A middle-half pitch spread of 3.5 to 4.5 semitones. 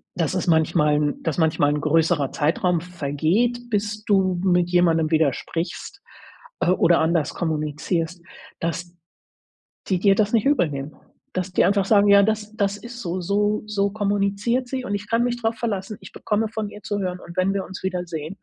Yes: average, 4.0 semitones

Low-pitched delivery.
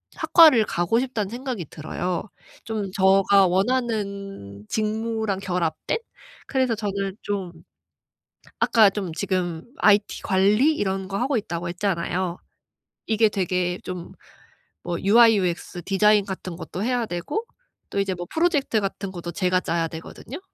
No: high, 195 Hz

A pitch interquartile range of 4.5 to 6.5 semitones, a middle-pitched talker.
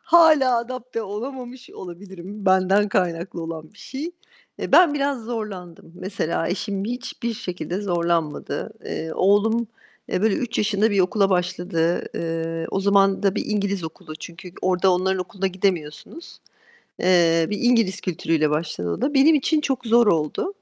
No: average, 5.1 semitones; high, 195 Hz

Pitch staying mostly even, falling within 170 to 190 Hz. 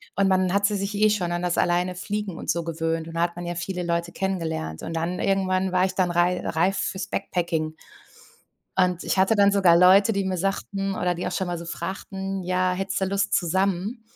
Yes: narrow, 2.0 semitones; medium, 185 Hz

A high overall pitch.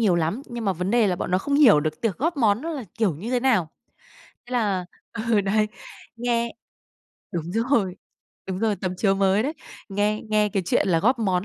Yes: high, 210 Hz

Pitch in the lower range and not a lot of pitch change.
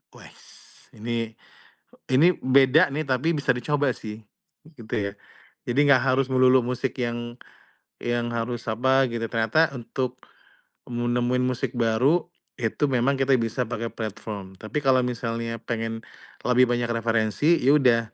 Yes: low, 120 Hz; narrow, 2.3 semitones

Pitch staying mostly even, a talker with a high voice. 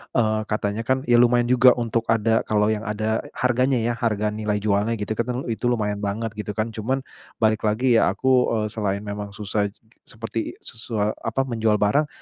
No: narrow, 2.2 semitones; low, 110 Hz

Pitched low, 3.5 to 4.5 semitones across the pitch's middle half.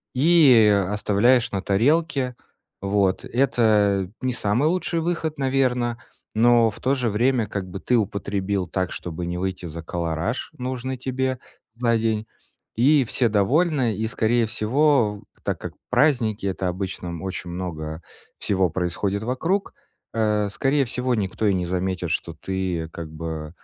No: low, 110 Hz; average, 5.2 semitones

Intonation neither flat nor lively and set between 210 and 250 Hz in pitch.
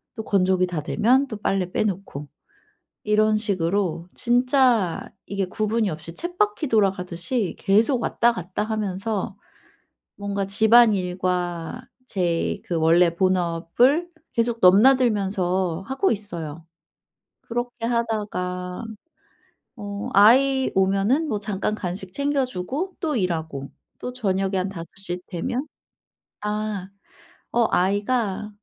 No: average, 4.3 semitones; high, 200 Hz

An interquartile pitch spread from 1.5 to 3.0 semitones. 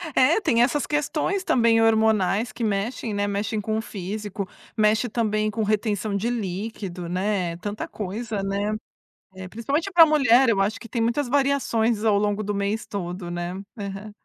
Yes: average, 2.7 semitones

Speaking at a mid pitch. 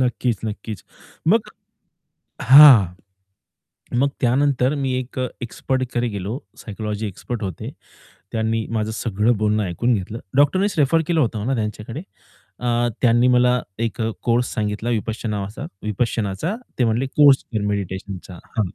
No: low, 115 Hz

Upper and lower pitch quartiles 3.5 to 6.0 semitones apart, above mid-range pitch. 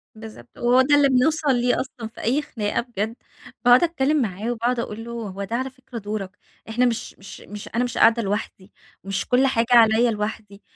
No: average, 3.0 semitones; high, 235 Hz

